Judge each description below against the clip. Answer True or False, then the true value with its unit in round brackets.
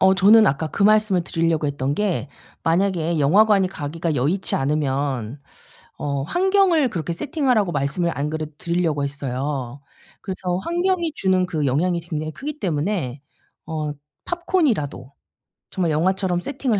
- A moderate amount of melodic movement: False (5.7 semitones)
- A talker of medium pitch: True (170 Hz)